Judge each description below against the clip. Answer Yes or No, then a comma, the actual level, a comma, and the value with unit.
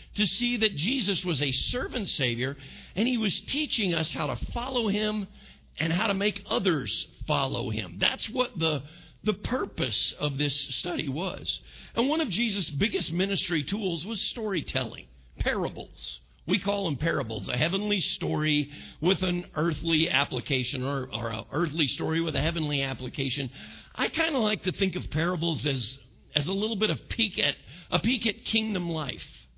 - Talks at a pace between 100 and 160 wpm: No, average, 170 wpm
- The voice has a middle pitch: Yes, medium, 165 Hz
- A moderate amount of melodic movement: No, wide, 6.5 semitones